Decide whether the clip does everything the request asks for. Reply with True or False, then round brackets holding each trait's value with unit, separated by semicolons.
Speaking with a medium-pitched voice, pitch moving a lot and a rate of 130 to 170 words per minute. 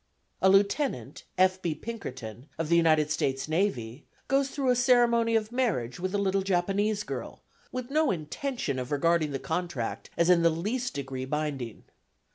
True (175 Hz; 7.6 semitones; 165 wpm)